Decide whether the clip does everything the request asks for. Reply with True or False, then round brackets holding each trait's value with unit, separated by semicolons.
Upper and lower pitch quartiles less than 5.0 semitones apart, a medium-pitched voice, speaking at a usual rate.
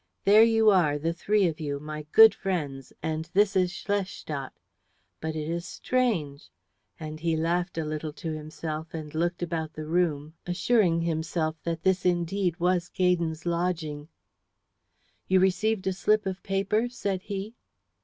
True (3.5 semitones; 170 Hz; 155 wpm)